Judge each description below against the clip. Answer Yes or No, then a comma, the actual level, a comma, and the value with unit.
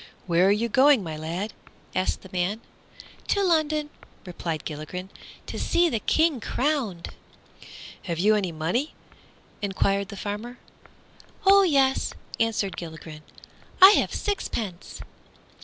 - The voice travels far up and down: Yes, wide, 7.9 semitones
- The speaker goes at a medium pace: No, slow, 125 wpm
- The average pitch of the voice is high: Yes, high, 205 Hz